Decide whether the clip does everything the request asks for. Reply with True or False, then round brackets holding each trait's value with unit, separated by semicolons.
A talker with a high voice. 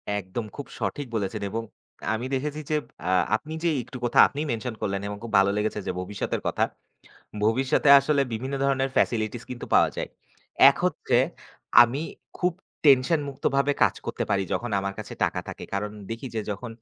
False (120 Hz)